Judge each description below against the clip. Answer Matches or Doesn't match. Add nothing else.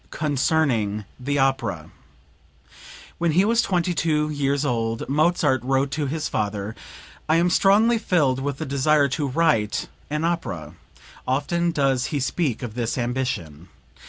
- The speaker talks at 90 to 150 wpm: Matches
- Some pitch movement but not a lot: Matches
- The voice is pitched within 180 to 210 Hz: Doesn't match